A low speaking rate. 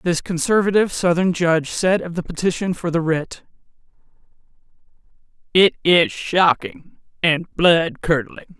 Yes: slow, 120 wpm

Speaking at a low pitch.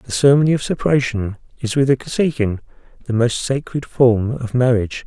Yes: low, 125 Hz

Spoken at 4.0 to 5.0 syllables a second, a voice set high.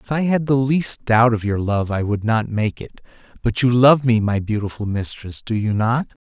No: 4.8 syllables/s; low, 115 Hz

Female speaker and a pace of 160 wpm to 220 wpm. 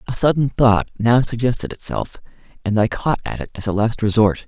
No: male; average, 200 wpm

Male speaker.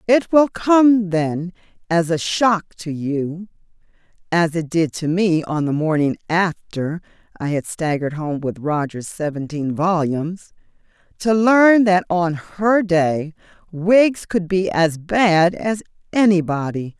No: female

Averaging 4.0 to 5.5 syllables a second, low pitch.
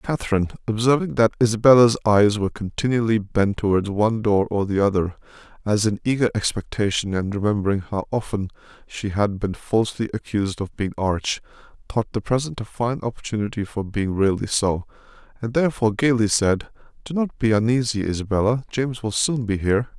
No: 5.8 syllables/s; low, 110 Hz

